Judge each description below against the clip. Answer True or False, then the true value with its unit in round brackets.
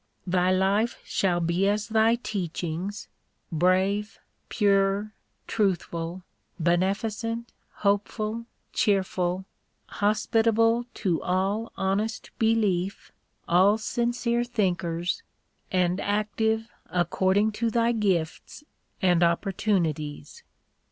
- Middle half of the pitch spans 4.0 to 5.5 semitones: False (3.5 semitones)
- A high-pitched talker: True (200 Hz)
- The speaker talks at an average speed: False (85 wpm)